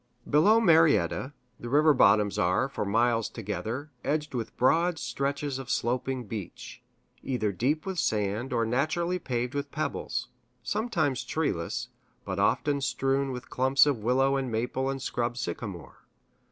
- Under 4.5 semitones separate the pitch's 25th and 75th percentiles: Yes, average, 4.0 semitones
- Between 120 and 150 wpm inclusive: Yes, average, 140 wpm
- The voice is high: No, low, 130 Hz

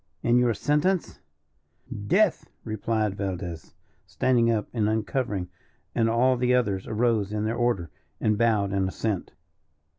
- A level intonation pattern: No, average, 3.3 semitones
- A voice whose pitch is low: Yes, low, 110 Hz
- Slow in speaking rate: Yes, slow, 130 wpm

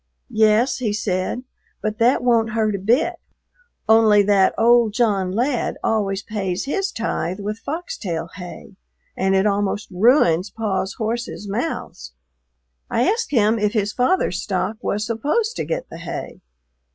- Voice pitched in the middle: No, high, 215 Hz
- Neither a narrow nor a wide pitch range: Yes, average, 3.4 semitones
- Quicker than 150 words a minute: No, average, 145 wpm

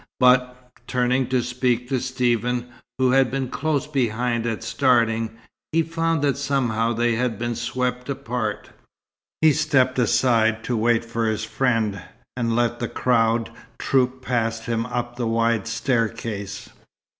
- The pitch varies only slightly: Yes, narrow, 2.0 semitones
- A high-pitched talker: No, low, 120 Hz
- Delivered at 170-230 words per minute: No, average, 145 wpm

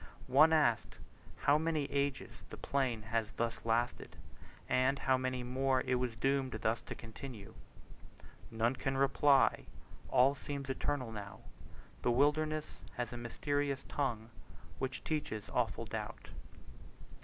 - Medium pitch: No, low, 130 Hz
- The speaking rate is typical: No, slow, 130 wpm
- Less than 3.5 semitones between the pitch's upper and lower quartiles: Yes, average, 3.1 semitones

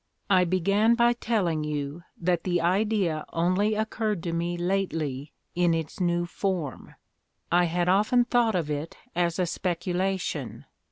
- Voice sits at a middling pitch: Yes, medium, 175 Hz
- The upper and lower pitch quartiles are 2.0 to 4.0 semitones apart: Yes, average, 3.1 semitones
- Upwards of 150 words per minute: No, average, 145 wpm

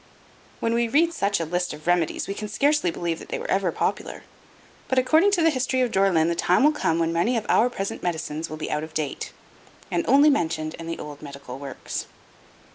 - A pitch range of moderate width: No, wide, 7.7 semitones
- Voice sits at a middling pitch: Yes, medium, 180 Hz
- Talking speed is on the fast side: Yes, fast, 225 wpm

